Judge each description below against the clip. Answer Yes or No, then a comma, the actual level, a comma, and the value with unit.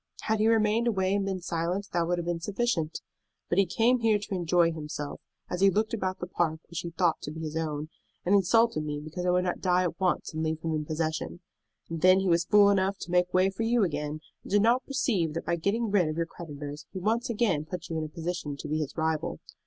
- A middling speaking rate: No, fast, 250 wpm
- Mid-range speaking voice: Yes, medium, 175 Hz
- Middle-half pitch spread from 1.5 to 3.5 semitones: No, average, 3.9 semitones